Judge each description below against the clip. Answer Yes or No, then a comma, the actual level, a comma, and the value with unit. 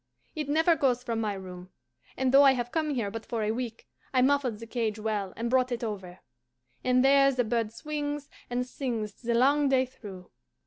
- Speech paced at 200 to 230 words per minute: Yes, fast, 205 wpm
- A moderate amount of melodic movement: Yes, average, 3.6 semitones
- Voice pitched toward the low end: No, high, 245 Hz